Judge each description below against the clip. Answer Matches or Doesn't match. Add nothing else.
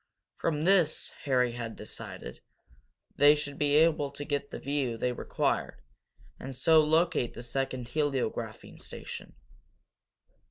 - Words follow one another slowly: Matches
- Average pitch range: Matches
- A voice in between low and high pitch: Matches